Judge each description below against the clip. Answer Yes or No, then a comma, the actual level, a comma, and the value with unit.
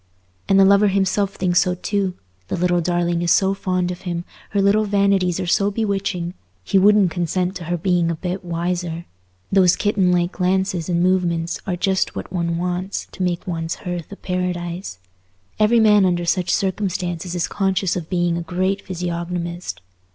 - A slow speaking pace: No, average, 175 wpm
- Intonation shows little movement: Yes, narrow, 1.8 semitones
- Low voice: No, medium, 180 Hz